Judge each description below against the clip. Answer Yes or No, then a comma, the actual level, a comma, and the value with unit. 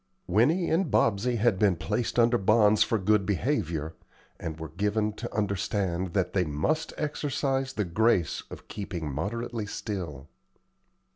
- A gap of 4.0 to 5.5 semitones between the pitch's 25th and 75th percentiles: Yes, average, 4.8 semitones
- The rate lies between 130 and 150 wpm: Yes, average, 140 wpm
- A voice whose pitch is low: Yes, low, 105 Hz